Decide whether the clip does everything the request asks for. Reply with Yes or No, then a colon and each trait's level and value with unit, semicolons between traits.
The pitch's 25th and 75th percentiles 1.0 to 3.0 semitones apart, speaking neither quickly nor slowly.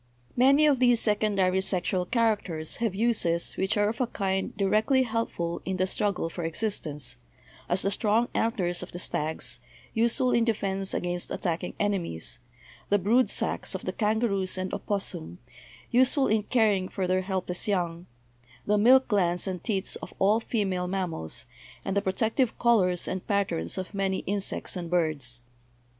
No: average, 3.6 semitones; average, 165 wpm